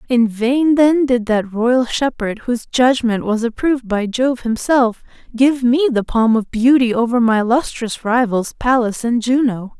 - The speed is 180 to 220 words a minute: No, average, 165 wpm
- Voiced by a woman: Yes, female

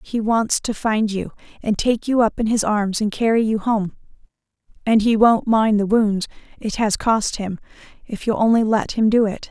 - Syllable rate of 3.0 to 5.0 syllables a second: Yes, 4.7 syllables/s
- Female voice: Yes, female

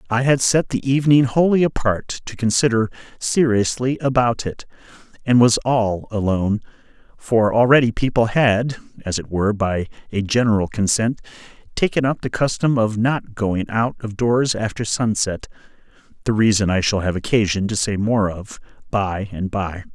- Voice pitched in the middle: No, low, 115 Hz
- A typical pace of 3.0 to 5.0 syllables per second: Yes, 4.9 syllables/s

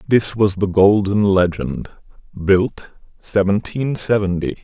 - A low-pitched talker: Yes, low, 100 Hz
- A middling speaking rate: No, slow, 105 wpm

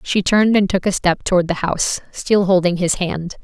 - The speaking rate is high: Yes, fast, 225 wpm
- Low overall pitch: No, medium, 185 Hz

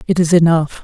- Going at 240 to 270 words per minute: No, fast, 215 wpm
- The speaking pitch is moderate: Yes, medium, 165 Hz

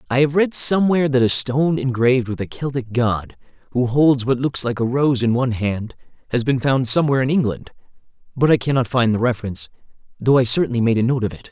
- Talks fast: Yes, fast, 220 wpm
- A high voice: No, low, 125 Hz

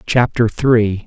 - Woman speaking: No, male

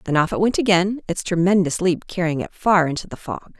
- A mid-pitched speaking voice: Yes, medium, 180 Hz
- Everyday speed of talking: No, fast, 235 wpm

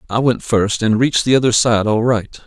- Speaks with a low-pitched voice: Yes, low, 115 Hz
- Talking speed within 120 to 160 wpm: No, fast, 245 wpm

